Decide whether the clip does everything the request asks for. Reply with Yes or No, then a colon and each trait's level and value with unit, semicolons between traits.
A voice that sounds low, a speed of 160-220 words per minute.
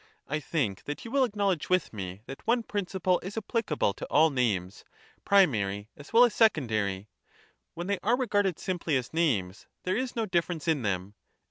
No: medium, 165 Hz; average, 180 wpm